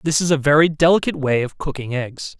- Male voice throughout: Yes, male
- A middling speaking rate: No, fast, 225 wpm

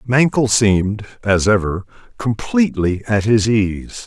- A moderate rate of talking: No, slow, 120 wpm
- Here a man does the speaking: Yes, male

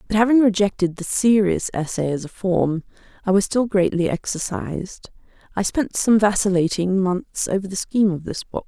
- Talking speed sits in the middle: Yes, average, 175 wpm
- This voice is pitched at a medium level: No, high, 195 Hz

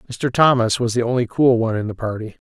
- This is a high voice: No, low, 120 Hz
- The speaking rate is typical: No, fast, 245 wpm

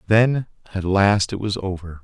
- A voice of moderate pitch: No, low, 100 Hz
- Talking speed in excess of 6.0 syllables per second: No, 4.5 syllables/s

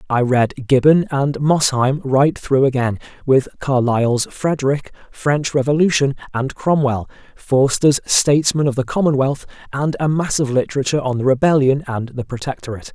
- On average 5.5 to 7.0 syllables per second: No, 5.0 syllables/s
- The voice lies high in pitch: No, low, 135 Hz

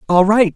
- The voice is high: Yes, high, 200 Hz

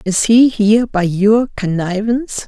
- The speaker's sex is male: No, female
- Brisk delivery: No, average, 145 wpm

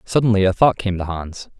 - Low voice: Yes, low, 100 Hz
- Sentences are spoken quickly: Yes, fast, 225 wpm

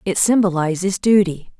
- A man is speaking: No, female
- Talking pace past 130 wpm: No, slow, 115 wpm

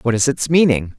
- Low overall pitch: Yes, low, 130 Hz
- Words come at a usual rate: No, fast, 245 wpm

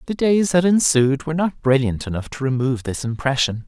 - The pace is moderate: Yes, average, 195 wpm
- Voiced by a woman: No, male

